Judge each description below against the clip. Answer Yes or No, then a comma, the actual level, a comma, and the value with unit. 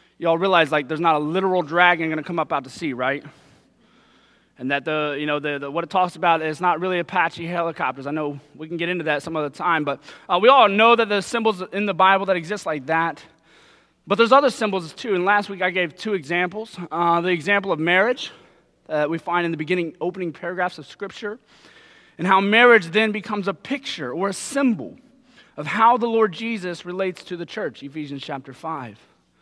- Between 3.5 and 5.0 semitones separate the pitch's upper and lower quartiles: Yes, average, 4.0 semitones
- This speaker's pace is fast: Yes, fast, 220 wpm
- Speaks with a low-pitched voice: No, medium, 180 Hz